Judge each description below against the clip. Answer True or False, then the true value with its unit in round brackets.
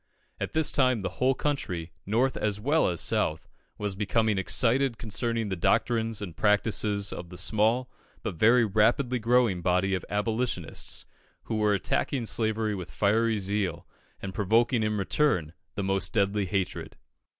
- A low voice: True (105 Hz)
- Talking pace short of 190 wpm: True (150 wpm)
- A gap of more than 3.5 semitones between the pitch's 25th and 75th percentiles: False (3.2 semitones)